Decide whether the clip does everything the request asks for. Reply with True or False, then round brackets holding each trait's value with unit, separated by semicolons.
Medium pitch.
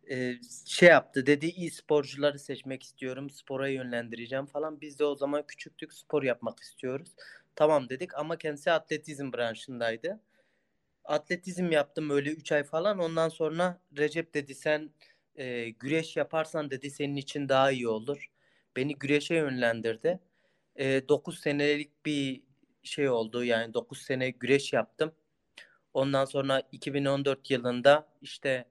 True (145 Hz)